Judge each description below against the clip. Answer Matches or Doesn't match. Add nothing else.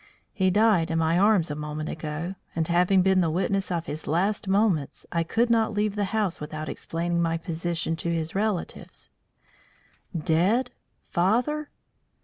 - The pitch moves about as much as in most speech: Matches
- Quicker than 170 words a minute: Doesn't match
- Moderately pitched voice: Matches